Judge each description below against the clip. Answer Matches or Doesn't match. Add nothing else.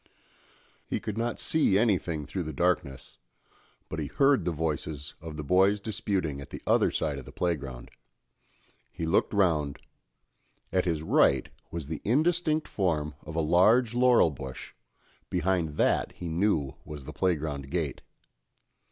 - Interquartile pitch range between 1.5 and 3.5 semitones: Doesn't match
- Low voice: Matches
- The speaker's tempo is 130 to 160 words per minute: Matches